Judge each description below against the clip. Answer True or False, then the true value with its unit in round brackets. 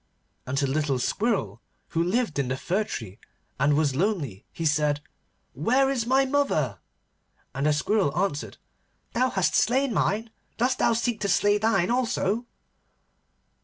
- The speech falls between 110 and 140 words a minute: False (155 wpm)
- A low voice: False (190 Hz)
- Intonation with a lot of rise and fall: True (8.2 semitones)